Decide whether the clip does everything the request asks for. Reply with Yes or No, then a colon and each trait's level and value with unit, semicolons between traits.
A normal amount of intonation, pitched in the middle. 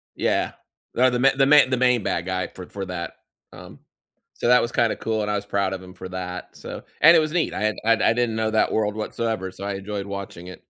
No: average, 4.4 semitones; low, 105 Hz